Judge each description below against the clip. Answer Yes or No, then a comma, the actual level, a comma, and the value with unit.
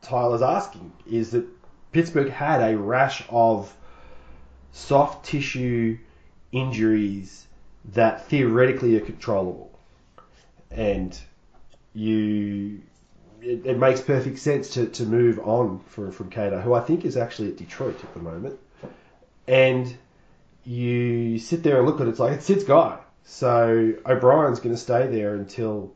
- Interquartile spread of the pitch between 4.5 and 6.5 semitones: No, average, 3.6 semitones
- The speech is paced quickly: No, average, 140 wpm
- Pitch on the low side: Yes, low, 120 Hz